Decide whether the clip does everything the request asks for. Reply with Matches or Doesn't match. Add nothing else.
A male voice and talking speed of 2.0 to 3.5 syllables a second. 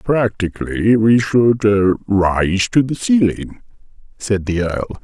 Matches